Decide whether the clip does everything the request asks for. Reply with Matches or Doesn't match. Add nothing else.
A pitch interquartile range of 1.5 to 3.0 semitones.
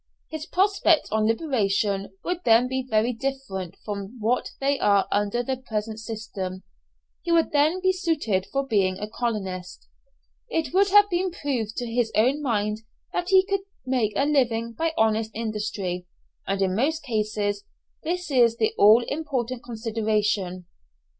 Doesn't match